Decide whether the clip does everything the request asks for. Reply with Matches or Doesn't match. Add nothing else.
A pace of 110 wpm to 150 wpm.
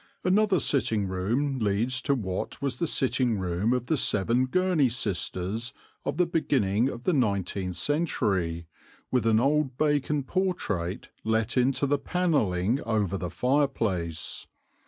Matches